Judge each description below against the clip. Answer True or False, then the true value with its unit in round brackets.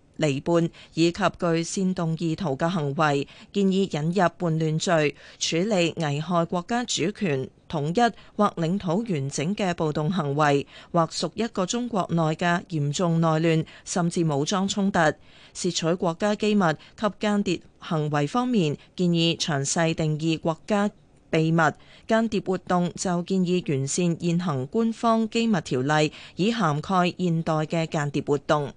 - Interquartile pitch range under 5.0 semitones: True (3.6 semitones)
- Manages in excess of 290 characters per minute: False (225 characters per minute)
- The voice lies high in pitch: False (170 Hz)